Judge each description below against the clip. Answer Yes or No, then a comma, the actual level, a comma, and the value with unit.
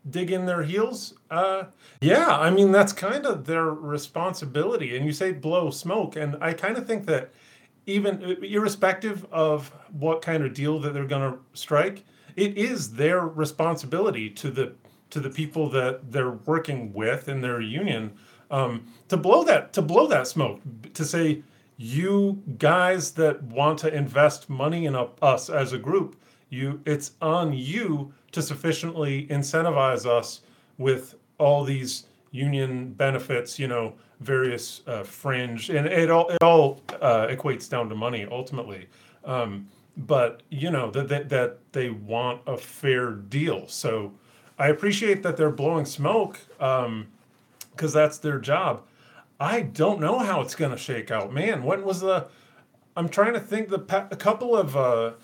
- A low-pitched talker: No, medium, 145 Hz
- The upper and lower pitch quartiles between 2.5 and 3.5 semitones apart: No, average, 4.6 semitones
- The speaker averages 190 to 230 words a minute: No, average, 165 wpm